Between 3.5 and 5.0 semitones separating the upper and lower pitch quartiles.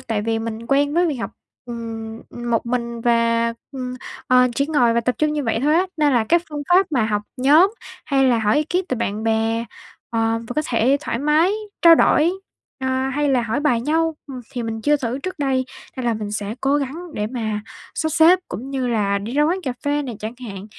Yes: average, 4.4 semitones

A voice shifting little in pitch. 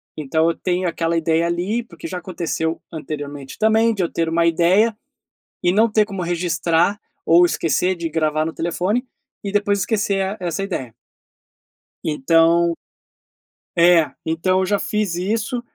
No: average, 3.4 semitones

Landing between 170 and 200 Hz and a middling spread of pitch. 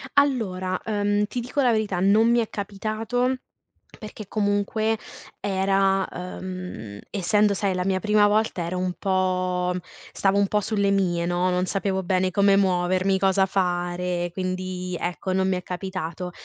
No: high, 190 Hz; narrow, 2.1 semitones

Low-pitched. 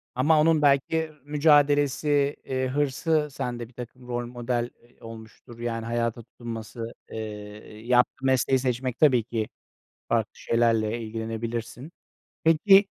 Yes: low, 125 Hz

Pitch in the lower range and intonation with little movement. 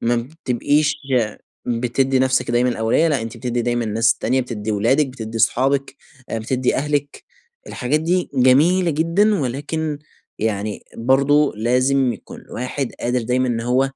No: low, 130 Hz; average, 3.4 semitones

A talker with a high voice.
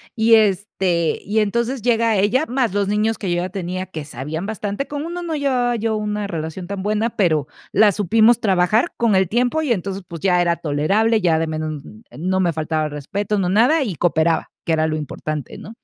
Yes: high, 200 Hz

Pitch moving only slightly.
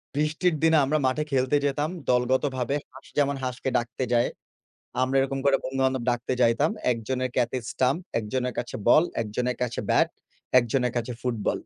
Yes: narrow, 1.8 semitones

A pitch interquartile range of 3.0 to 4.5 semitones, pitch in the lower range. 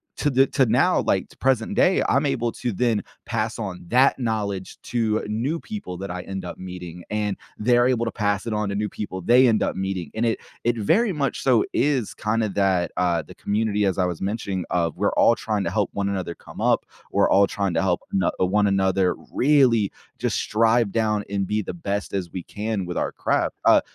Yes: average, 3.5 semitones; low, 105 Hz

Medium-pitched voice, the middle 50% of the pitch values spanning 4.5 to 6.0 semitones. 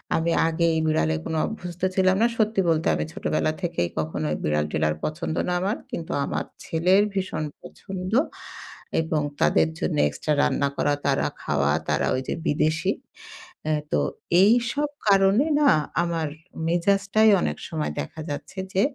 Yes: medium, 165 Hz; average, 5.2 semitones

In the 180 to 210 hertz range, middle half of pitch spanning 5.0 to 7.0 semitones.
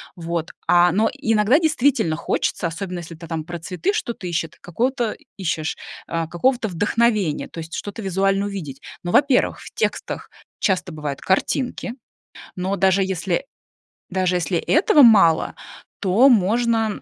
Yes: high, 190 Hz; wide, 5.5 semitones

